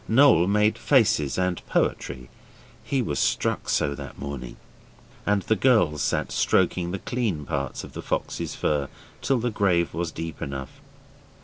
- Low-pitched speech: Yes, very low, 85 Hz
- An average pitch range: No, wide, 7.2 semitones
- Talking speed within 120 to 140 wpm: No, average, 150 wpm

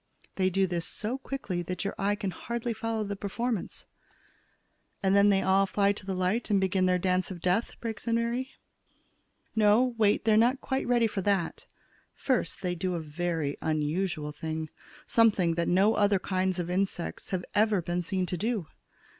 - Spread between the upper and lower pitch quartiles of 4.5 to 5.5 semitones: No, average, 3.5 semitones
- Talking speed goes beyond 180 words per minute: Yes, average, 190 wpm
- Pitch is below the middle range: No, high, 195 Hz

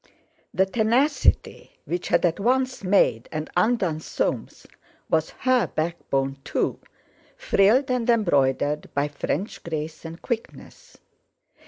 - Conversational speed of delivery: No, slow, 115 wpm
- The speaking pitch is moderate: Yes, medium, 180 Hz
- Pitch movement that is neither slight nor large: No, wide, 7.5 semitones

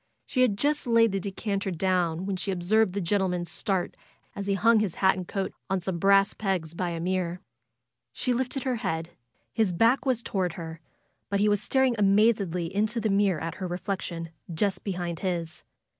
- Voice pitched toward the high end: Yes, high, 195 Hz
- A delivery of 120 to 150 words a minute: No, average, 190 wpm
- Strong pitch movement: No, average, 3.3 semitones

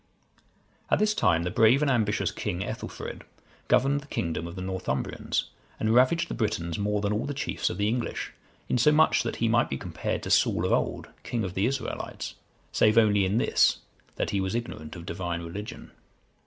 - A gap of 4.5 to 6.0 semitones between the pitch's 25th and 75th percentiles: Yes, average, 5.0 semitones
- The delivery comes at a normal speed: Yes, average, 195 wpm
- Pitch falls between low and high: No, low, 105 Hz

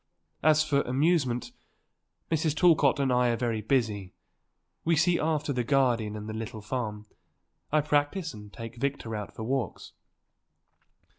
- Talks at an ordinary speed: Yes, average, 145 wpm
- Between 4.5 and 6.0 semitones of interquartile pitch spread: Yes, average, 5.1 semitones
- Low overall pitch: Yes, low, 130 Hz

